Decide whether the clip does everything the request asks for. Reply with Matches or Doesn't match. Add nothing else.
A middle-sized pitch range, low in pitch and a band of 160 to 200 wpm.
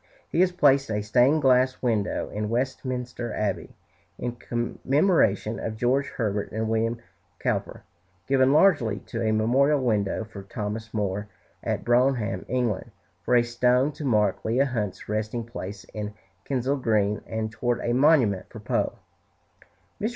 Doesn't match